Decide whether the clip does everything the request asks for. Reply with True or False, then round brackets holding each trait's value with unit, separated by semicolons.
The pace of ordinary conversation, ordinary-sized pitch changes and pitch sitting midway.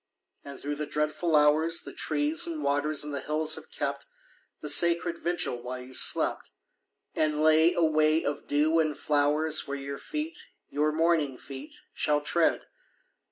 False (160 wpm; 2.2 semitones; 155 Hz)